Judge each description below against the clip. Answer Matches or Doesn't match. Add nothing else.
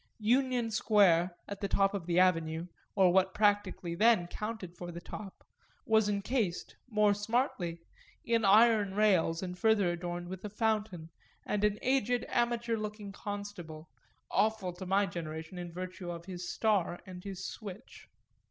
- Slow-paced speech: Doesn't match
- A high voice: Matches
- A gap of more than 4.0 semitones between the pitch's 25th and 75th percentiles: Doesn't match